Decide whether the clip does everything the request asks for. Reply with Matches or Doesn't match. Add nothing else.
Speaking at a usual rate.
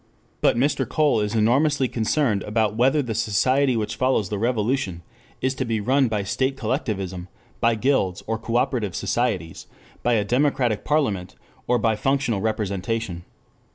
Matches